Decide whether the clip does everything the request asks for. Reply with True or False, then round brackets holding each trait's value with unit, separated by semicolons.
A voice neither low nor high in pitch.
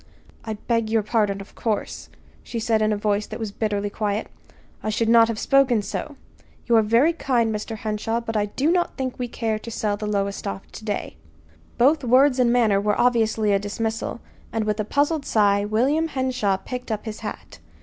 False (220 Hz)